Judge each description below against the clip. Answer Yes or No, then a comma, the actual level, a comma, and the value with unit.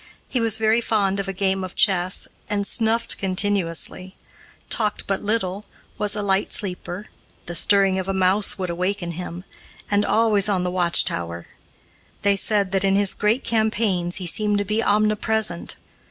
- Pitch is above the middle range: Yes, high, 200 Hz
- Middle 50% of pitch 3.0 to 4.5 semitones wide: No, narrow, 2.4 semitones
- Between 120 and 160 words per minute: No, average, 170 wpm